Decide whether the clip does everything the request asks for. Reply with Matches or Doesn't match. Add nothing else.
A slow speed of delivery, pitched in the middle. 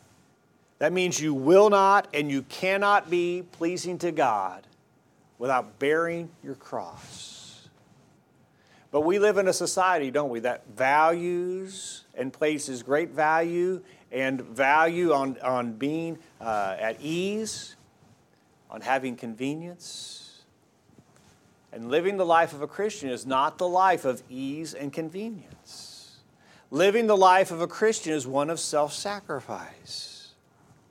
Matches